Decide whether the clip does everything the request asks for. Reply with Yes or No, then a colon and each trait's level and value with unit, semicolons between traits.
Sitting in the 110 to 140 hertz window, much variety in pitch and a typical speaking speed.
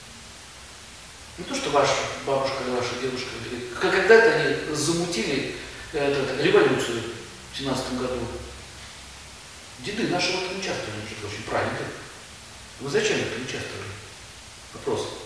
No: low, 135 Hz; wide, 6.5 semitones; slow, 105 wpm